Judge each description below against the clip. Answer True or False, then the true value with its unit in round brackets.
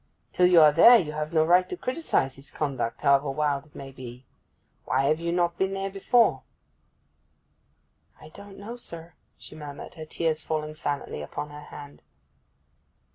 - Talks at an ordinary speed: True (170 wpm)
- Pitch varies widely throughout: False (4.0 semitones)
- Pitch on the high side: False (155 Hz)